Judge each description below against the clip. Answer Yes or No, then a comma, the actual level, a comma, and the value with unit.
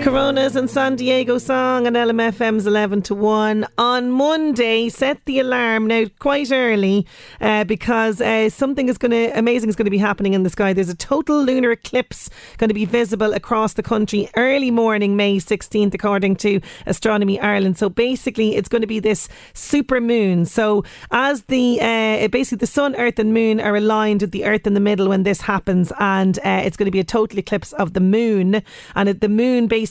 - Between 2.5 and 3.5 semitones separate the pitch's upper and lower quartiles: Yes, average, 3.0 semitones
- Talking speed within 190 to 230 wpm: Yes, average, 200 wpm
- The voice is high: Yes, high, 220 Hz